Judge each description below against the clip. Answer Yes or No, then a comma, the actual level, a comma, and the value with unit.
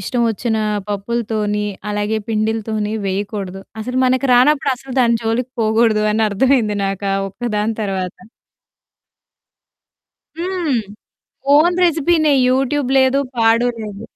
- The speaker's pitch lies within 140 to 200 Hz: No, high, 225 Hz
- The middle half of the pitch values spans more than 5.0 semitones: No, average, 3.7 semitones